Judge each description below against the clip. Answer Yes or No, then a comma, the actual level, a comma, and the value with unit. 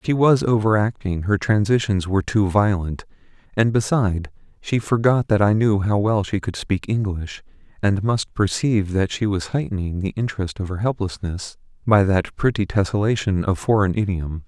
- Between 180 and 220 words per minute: No, average, 170 wpm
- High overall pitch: No, low, 100 Hz